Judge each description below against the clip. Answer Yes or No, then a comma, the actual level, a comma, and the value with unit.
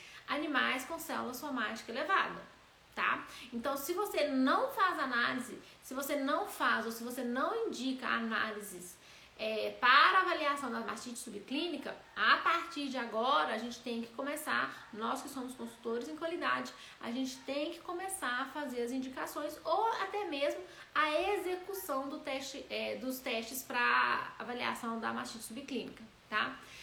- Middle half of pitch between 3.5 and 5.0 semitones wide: Yes, average, 4.3 semitones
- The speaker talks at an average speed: Yes, average, 150 wpm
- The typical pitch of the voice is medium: No, very high, 270 Hz